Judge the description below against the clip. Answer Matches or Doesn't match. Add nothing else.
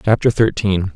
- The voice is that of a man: Matches